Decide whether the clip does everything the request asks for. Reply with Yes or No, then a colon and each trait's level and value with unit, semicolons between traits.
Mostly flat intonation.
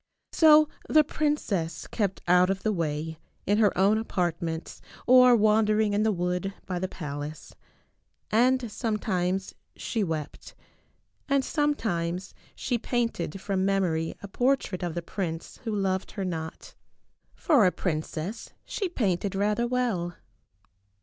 No: average, 4.6 semitones